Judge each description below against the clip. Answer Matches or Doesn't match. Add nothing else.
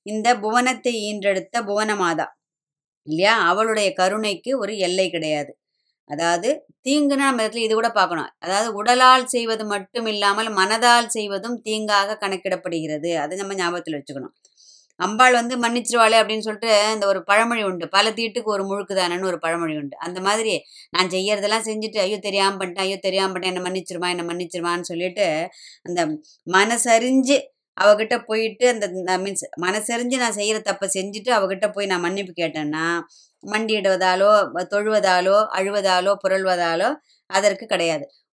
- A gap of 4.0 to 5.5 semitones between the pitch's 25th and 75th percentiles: Doesn't match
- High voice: Matches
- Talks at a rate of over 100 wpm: Matches